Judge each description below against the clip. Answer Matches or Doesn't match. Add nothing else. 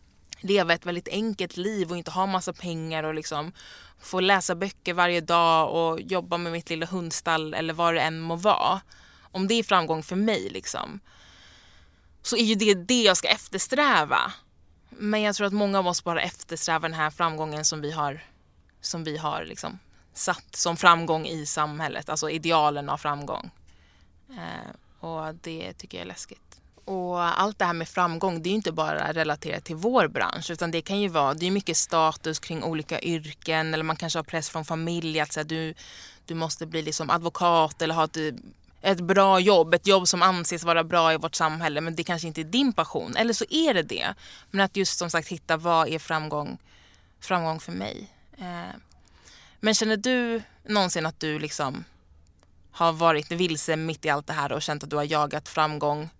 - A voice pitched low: Doesn't match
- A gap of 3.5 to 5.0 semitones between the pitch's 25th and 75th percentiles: Doesn't match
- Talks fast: Doesn't match